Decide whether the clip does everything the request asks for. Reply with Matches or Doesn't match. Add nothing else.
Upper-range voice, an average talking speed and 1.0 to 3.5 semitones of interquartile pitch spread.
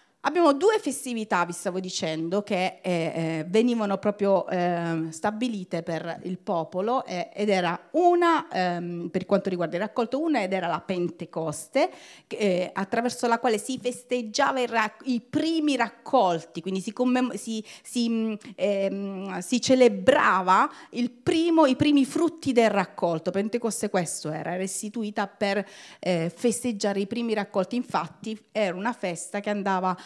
Doesn't match